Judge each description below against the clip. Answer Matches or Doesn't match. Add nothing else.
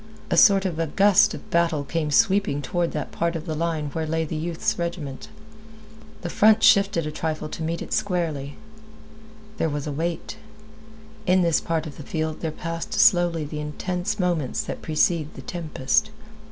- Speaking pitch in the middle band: Matches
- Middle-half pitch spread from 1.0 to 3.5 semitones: Matches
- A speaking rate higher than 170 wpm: Matches